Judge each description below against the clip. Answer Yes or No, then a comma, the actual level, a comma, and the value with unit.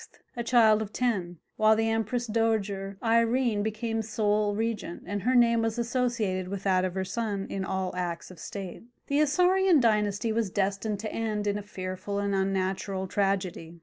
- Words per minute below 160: No, average, 175 wpm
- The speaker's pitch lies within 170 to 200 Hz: No, high, 210 Hz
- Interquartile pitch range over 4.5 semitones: No, average, 2.9 semitones